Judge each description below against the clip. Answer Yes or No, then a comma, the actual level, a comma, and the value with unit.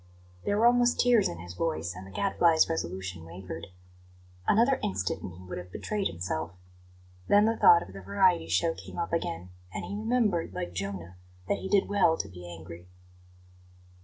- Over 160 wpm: Yes, average, 180 wpm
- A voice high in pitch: No, very low, 95 Hz